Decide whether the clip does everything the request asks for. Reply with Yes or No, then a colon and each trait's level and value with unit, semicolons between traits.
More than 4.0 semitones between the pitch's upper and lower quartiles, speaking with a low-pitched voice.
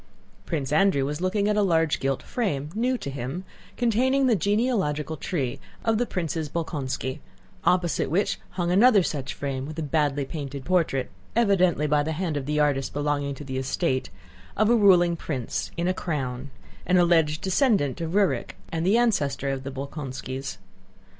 No: average, 5.3 semitones; medium, 160 Hz